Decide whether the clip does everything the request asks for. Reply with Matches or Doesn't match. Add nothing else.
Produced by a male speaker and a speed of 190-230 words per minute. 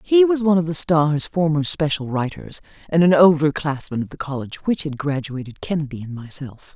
Doesn't match